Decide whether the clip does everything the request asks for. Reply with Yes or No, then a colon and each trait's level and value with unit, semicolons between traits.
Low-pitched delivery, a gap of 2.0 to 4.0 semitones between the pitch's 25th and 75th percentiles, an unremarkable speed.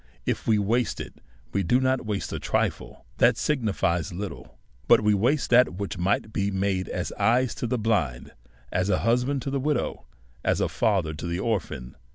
No: low, 105 Hz; average, 4.6 semitones; average, 195 wpm